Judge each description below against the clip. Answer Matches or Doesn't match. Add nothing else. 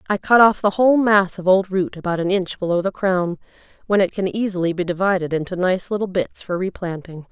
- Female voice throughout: Matches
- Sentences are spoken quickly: Matches